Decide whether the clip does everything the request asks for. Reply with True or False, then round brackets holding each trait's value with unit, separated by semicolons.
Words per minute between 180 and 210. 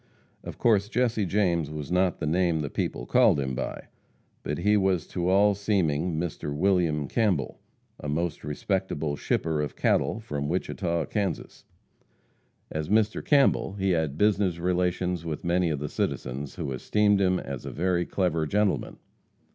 False (155 wpm)